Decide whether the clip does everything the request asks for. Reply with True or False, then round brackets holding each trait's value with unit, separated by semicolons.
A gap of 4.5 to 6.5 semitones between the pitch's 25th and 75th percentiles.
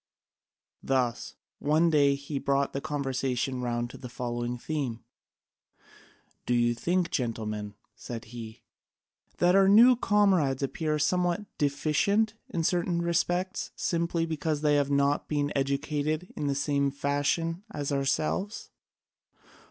False (4.1 semitones)